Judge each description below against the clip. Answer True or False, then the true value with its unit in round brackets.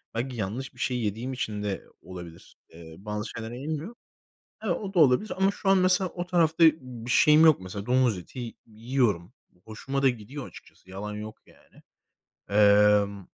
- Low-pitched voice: True (120 Hz)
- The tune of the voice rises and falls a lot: True (6.0 semitones)